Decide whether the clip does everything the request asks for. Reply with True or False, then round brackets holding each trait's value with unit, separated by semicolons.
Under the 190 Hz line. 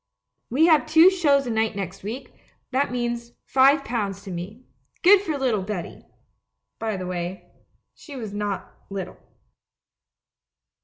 False (235 Hz)